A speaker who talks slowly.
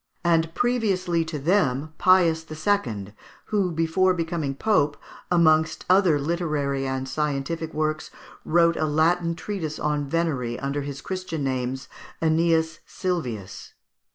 Yes: slow, 120 wpm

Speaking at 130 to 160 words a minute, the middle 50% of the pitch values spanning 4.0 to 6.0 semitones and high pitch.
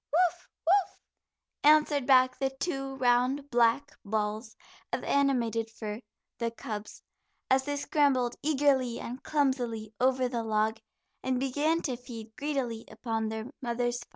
No: slow, 135 wpm; average, 3.6 semitones; very high, 255 Hz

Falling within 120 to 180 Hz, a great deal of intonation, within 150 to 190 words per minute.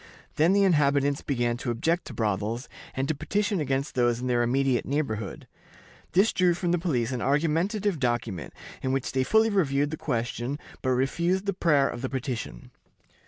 Yes: medium, 140 Hz; wide, 5.8 semitones; average, 175 wpm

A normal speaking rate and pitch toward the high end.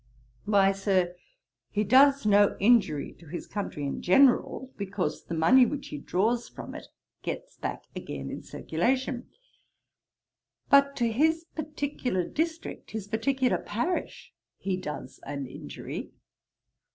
No: slow, 125 wpm; high, 215 Hz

